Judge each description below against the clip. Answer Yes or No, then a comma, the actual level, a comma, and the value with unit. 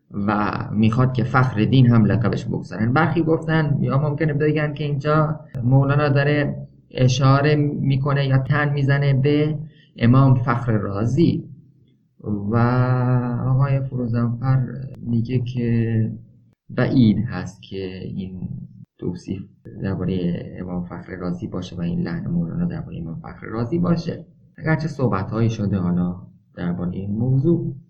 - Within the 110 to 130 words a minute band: Yes, average, 125 wpm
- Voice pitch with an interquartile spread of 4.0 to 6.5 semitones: Yes, average, 5.2 semitones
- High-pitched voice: No, low, 130 Hz